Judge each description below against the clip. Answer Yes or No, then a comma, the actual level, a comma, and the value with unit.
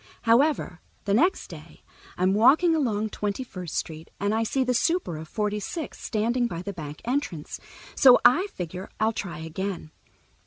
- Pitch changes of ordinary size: No, wide, 5.8 semitones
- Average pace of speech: Yes, average, 165 wpm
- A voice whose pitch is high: Yes, high, 210 Hz